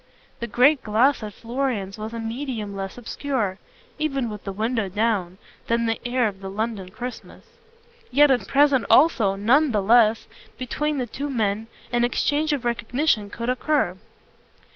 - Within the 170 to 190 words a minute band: No, average, 160 wpm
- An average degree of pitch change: Yes, average, 3.9 semitones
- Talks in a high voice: Yes, high, 235 Hz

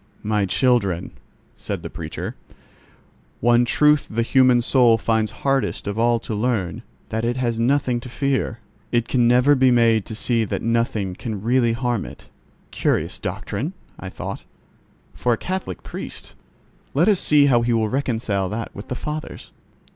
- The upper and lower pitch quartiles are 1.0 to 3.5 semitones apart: Yes, narrow, 2.6 semitones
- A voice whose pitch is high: No, low, 120 Hz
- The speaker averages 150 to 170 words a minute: Yes, average, 160 wpm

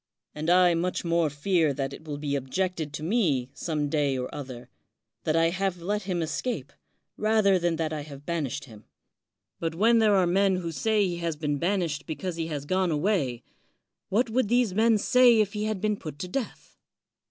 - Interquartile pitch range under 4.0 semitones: No, average, 5.2 semitones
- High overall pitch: No, medium, 170 Hz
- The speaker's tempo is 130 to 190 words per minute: No, average, 200 wpm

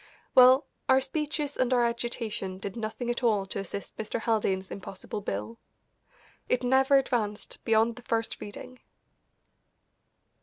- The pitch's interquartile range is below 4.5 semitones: Yes, average, 3.8 semitones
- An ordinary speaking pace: No, slow, 130 wpm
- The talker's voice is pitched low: No, high, 230 Hz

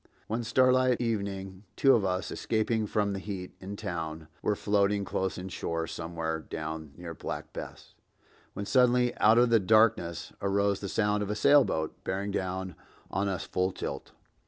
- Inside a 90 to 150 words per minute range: No, average, 160 wpm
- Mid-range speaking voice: No, low, 100 Hz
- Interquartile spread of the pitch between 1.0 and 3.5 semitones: Yes, average, 3.1 semitones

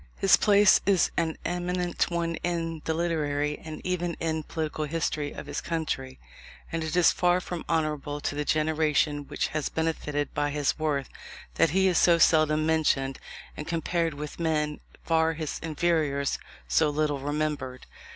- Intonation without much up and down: Yes, narrow, 2.1 semitones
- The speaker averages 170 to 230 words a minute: No, average, 160 wpm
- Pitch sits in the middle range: Yes, medium, 155 Hz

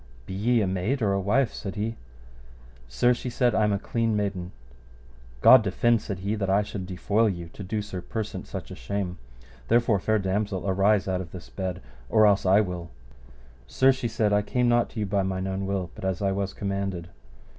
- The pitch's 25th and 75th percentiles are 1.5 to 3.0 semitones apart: Yes, narrow, 2.5 semitones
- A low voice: Yes, low, 100 Hz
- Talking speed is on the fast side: Yes, fast, 210 wpm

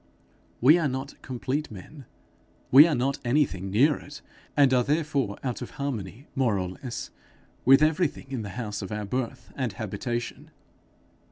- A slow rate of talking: No, average, 160 wpm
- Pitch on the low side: Yes, low, 130 Hz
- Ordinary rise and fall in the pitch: Yes, average, 4.5 semitones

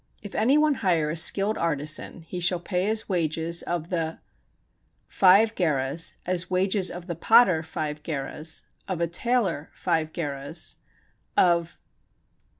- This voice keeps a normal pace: Yes, average, 145 wpm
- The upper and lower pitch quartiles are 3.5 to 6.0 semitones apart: No, average, 3.1 semitones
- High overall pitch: No, medium, 170 Hz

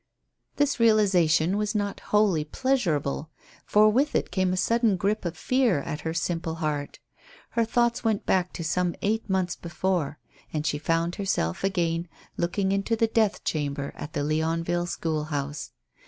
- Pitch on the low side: No, medium, 175 Hz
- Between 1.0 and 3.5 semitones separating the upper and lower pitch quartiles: No, average, 4.9 semitones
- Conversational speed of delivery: Yes, average, 160 wpm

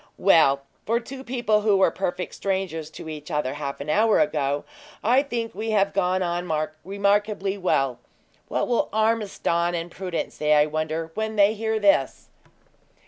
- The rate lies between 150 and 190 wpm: Yes, average, 165 wpm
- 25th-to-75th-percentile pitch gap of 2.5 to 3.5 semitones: No, wide, 5.4 semitones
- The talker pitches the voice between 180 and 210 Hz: Yes, high, 190 Hz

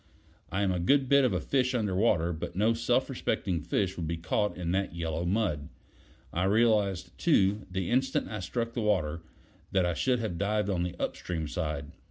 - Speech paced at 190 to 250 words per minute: Yes, average, 200 wpm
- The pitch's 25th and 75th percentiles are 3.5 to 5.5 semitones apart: Yes, average, 4.3 semitones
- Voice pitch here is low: Yes, very low, 95 Hz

